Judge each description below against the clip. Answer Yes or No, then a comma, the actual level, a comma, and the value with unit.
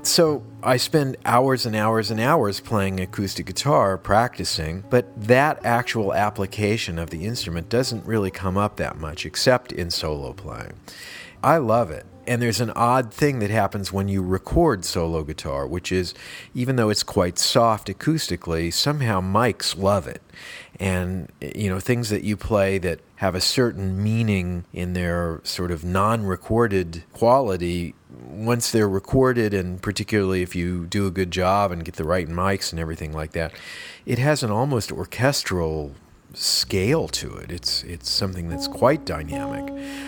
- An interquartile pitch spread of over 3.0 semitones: Yes, average, 4.7 semitones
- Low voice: Yes, low, 100 Hz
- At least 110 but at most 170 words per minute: Yes, average, 160 wpm